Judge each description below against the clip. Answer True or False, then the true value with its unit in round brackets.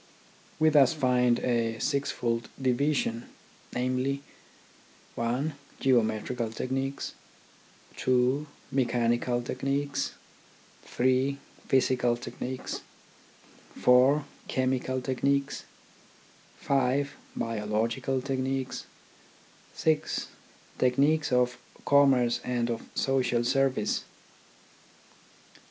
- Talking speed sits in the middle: False (75 wpm)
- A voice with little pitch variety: True (2.1 semitones)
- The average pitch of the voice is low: True (130 Hz)